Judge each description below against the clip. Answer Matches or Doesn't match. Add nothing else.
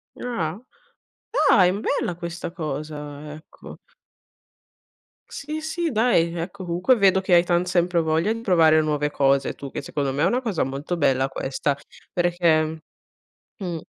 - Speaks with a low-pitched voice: Doesn't match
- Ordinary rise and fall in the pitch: Matches